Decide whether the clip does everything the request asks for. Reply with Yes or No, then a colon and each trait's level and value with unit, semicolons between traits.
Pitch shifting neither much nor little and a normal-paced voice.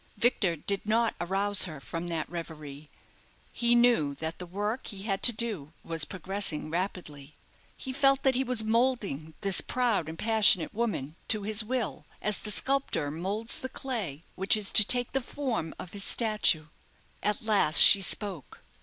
No: wide, 5.9 semitones; average, 170 wpm